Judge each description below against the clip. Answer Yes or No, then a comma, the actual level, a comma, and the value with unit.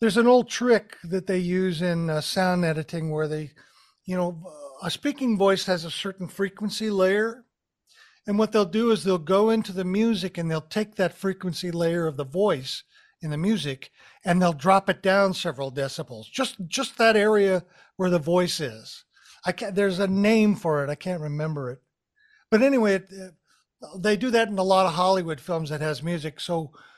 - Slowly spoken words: No, average, 195 wpm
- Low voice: No, medium, 185 Hz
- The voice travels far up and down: No, average, 4.1 semitones